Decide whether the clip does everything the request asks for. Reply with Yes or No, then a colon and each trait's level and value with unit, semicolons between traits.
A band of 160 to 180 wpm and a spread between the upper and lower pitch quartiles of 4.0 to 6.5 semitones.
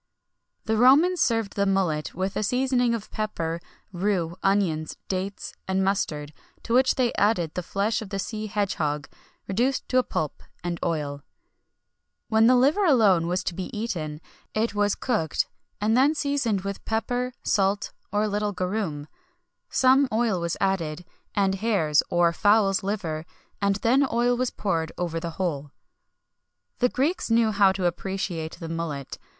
Yes: average, 165 wpm; average, 5.1 semitones